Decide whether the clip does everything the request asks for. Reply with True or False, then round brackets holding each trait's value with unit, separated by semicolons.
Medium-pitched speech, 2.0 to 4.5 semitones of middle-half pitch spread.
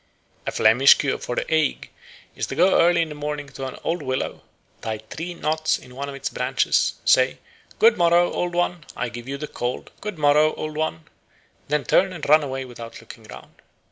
True (150 Hz; 3.9 semitones)